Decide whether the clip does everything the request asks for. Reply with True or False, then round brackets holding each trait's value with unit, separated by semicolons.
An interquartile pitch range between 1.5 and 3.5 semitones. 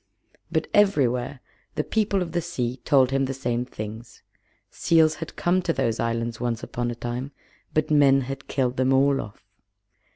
False (4.2 semitones)